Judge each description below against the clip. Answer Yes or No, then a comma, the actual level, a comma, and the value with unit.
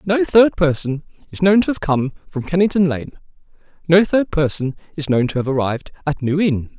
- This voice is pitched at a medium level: Yes, medium, 160 Hz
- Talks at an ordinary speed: Yes, average, 195 wpm